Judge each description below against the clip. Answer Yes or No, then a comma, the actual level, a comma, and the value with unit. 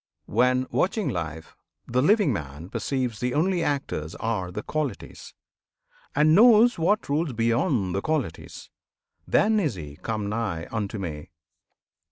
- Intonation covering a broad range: Yes, wide, 8.5 semitones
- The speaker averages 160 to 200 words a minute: No, slow, 135 wpm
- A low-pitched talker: Yes, low, 125 Hz